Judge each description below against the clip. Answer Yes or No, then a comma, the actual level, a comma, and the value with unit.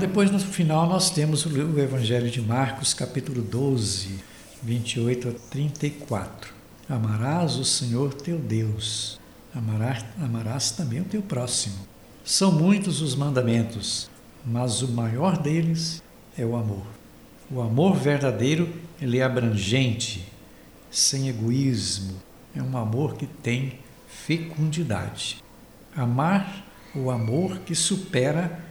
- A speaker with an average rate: No, slow, 115 wpm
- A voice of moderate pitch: No, low, 130 Hz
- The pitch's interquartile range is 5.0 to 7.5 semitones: Yes, wide, 5.4 semitones